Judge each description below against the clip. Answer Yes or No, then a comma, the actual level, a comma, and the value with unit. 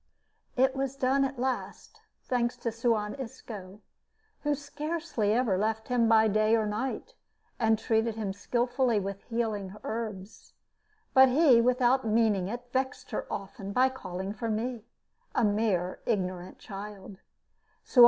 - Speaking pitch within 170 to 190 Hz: No, high, 225 Hz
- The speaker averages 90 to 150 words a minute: Yes, slow, 135 wpm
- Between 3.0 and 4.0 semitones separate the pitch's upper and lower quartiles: Yes, average, 3.4 semitones